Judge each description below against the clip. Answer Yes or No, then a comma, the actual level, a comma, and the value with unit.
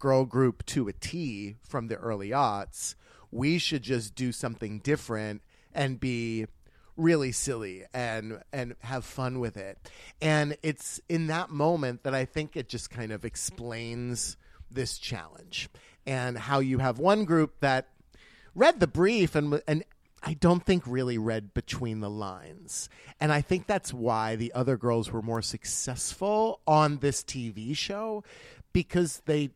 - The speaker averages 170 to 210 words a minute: No, average, 155 wpm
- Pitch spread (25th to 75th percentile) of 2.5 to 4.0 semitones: No, average, 4.9 semitones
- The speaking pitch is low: Yes, low, 130 Hz